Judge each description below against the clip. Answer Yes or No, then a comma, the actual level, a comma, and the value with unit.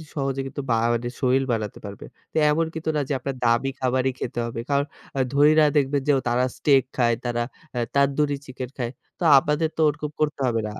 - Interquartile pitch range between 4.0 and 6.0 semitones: No, average, 3.3 semitones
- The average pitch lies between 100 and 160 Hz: Yes, low, 135 Hz